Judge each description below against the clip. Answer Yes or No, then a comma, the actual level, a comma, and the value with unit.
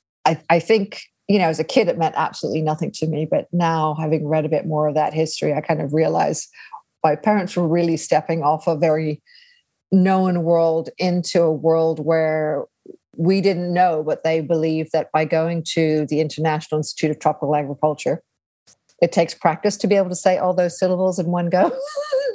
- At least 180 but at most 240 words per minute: Yes, average, 190 wpm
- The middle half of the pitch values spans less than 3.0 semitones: Yes, narrow, 2.6 semitones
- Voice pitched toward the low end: No, medium, 165 Hz